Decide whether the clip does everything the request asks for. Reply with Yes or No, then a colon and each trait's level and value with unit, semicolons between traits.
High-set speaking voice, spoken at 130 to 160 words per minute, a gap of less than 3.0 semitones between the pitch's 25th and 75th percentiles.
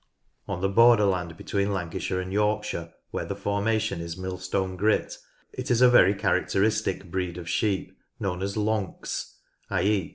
No: low, 100 Hz; average, 150 wpm; narrow, 2.5 semitones